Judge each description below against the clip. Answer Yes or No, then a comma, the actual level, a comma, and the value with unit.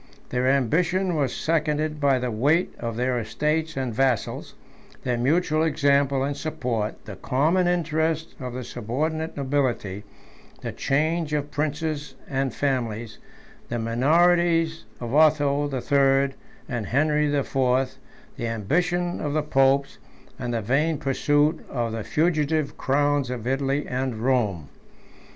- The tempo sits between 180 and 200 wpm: No, slow, 135 wpm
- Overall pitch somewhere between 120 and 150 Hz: Yes, medium, 140 Hz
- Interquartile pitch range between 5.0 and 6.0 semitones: No, average, 3.7 semitones